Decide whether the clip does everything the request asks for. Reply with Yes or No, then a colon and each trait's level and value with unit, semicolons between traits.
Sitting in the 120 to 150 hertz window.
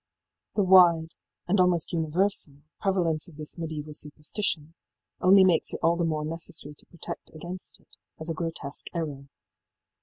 No: medium, 165 Hz